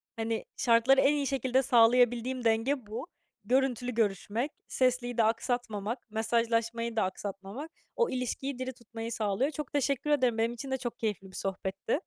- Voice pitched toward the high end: Yes, high, 235 Hz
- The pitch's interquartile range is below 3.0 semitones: Yes, narrow, 2.6 semitones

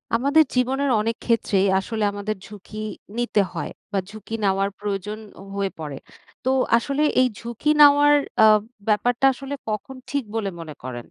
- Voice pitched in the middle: No, high, 215 Hz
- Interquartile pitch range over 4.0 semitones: Yes, average, 4.6 semitones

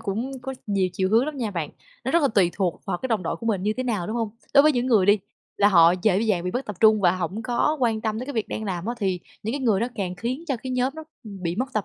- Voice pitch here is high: Yes, high, 215 Hz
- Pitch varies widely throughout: No, average, 4.6 semitones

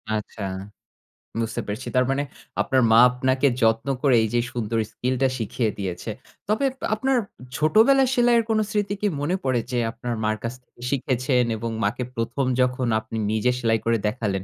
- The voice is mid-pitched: No, low, 125 Hz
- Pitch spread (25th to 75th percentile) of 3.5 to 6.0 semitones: Yes, average, 3.9 semitones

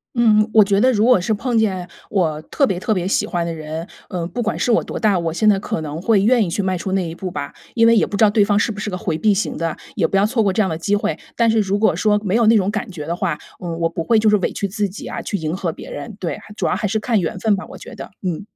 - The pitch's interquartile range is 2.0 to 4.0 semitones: Yes, average, 3.7 semitones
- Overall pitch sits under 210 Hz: Yes, high, 200 Hz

